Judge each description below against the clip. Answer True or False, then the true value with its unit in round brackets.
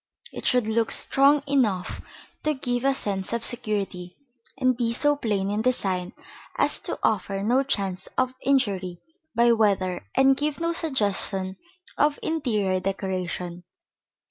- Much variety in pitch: True (5.7 semitones)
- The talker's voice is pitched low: False (220 Hz)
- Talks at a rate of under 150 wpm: True (140 wpm)